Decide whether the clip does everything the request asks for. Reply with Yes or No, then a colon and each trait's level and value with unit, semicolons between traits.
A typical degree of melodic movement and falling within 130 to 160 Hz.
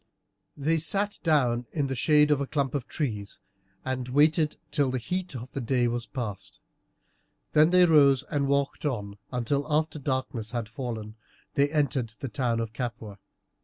Yes: average, 3.9 semitones; low, 135 Hz